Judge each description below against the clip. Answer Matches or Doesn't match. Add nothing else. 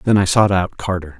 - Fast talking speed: Matches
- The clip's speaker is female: Doesn't match